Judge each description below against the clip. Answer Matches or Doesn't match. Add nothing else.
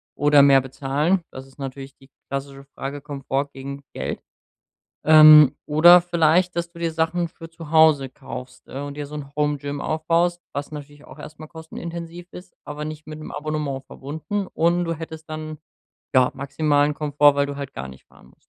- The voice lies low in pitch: Doesn't match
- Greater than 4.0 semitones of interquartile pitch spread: Doesn't match